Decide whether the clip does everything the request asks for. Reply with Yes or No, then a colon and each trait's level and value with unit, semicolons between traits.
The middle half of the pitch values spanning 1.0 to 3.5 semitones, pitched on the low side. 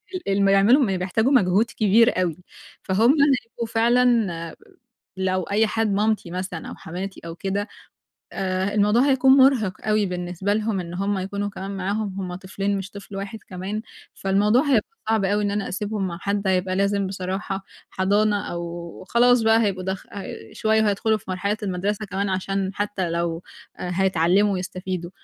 No: narrow, 2.5 semitones; high, 200 Hz